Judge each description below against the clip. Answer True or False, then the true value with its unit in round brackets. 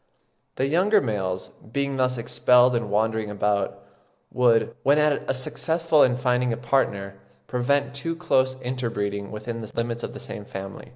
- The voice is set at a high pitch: False (125 Hz)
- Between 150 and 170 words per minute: True (160 wpm)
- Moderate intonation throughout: True (4.3 semitones)